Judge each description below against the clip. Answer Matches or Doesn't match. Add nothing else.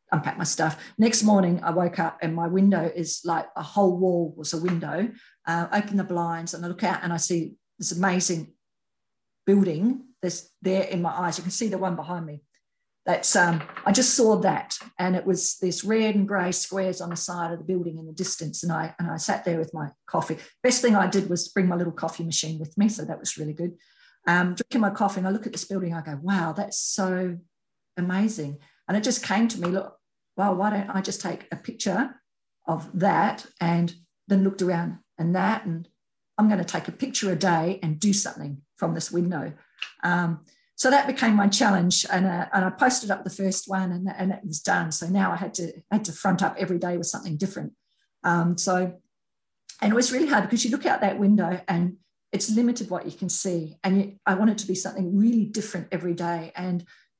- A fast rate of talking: Matches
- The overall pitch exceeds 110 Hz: Matches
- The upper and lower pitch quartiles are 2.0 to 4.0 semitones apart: Matches